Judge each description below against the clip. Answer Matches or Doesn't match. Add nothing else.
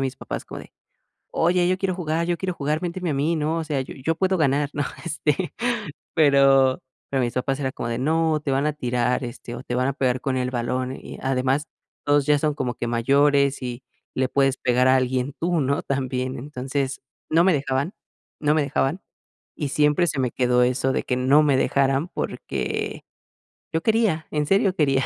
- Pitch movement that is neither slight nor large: Matches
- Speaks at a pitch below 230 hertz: Matches